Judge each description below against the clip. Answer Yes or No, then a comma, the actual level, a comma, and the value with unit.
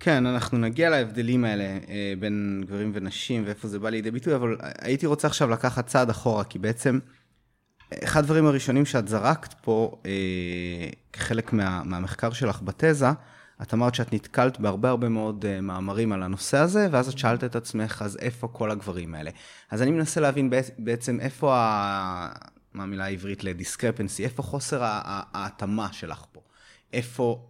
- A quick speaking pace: Yes, fast, 160 wpm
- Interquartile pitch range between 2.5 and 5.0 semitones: Yes, average, 4.2 semitones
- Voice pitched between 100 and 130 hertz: Yes, low, 115 Hz